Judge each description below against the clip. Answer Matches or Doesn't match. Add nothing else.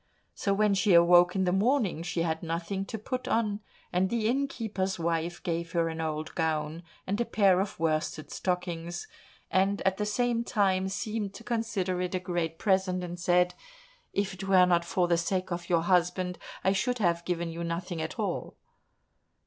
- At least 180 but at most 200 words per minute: Matches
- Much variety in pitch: Doesn't match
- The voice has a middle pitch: Matches